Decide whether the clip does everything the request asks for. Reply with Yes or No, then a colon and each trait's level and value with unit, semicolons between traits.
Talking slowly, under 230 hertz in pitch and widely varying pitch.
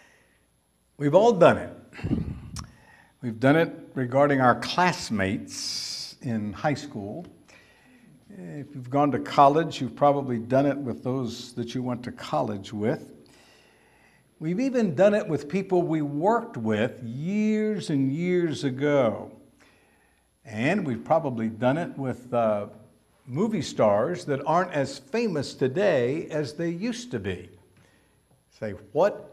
Yes: slow, 130 wpm; medium, 140 Hz; wide, 5.8 semitones